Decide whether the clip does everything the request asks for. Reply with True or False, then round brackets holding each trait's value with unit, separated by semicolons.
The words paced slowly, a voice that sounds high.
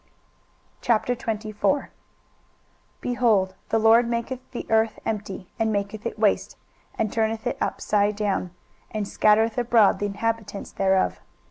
True (120 wpm; 220 Hz)